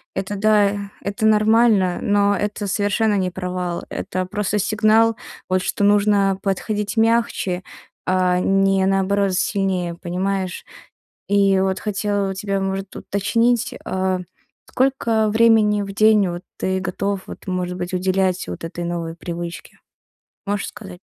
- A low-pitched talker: No, high, 195 Hz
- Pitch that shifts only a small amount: Yes, narrow, 2.1 semitones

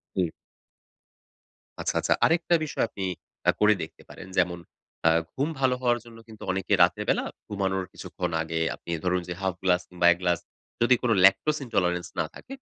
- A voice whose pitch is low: Yes, very low, 95 Hz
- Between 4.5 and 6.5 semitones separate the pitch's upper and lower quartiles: Yes, average, 5.2 semitones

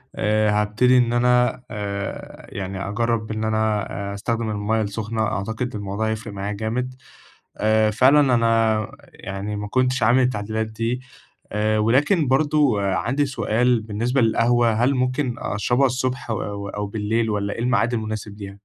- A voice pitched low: Yes, low, 110 Hz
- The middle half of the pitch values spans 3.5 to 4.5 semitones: No, average, 2.8 semitones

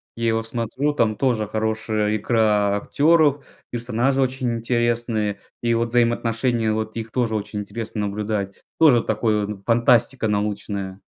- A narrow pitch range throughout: Yes, narrow, 2.1 semitones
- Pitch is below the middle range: Yes, low, 115 Hz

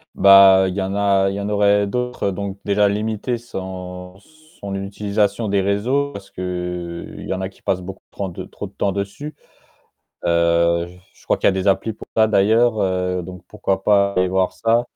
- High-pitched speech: No, low, 100 Hz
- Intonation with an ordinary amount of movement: No, narrow, 1.9 semitones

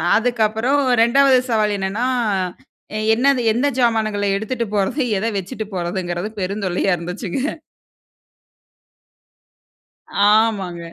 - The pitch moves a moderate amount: Yes, average, 3.8 semitones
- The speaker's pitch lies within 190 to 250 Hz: Yes, high, 215 Hz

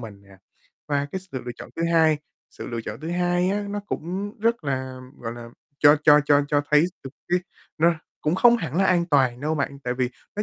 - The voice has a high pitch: No, medium, 150 Hz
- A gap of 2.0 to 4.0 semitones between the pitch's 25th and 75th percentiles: No, average, 5.2 semitones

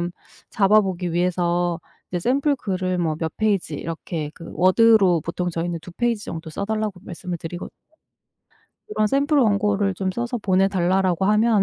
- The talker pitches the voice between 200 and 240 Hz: No, medium, 185 Hz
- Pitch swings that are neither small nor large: Yes, average, 3.5 semitones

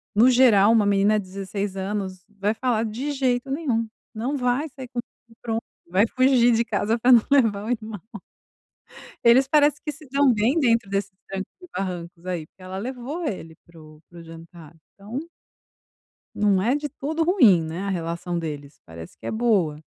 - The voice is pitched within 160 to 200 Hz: No, high, 215 Hz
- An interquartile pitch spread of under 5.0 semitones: No, average, 5.3 semitones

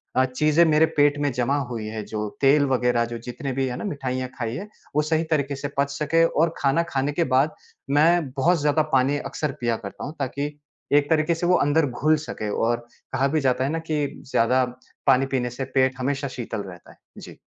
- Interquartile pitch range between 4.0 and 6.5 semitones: No, average, 3.1 semitones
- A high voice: No, medium, 140 Hz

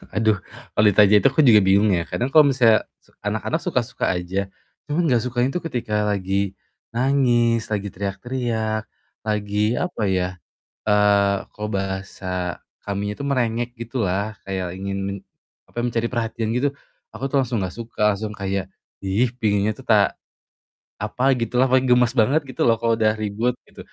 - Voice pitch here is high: No, low, 110 Hz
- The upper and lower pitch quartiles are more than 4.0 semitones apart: No, average, 3.3 semitones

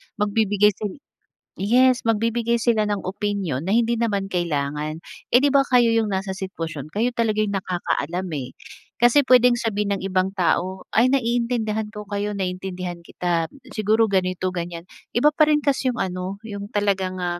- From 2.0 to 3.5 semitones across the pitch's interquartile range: No, average, 4.0 semitones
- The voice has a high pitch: Yes, high, 205 Hz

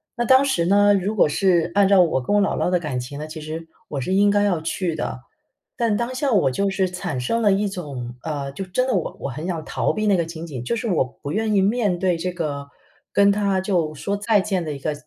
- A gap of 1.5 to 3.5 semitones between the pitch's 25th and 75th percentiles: No, average, 4.7 semitones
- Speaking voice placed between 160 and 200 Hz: Yes, medium, 185 Hz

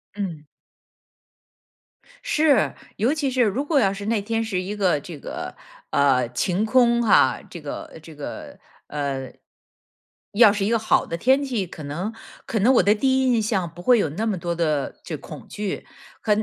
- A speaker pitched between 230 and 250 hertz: No, high, 205 Hz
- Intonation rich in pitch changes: Yes, wide, 5.8 semitones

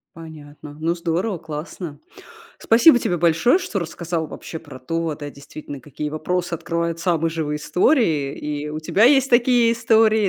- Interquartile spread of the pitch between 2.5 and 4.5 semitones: No, average, 5.3 semitones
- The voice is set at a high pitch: No, medium, 165 Hz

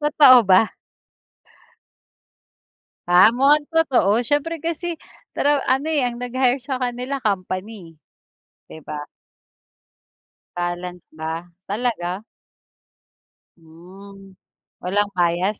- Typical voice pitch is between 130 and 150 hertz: No, high, 215 Hz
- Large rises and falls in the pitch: Yes, wide, 6.8 semitones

